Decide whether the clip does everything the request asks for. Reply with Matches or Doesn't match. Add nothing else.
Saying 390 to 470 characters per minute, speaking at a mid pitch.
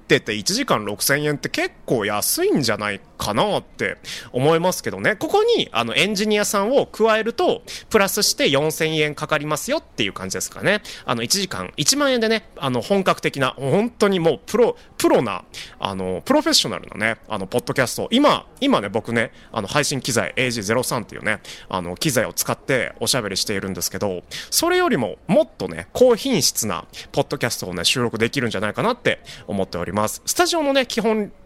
Matches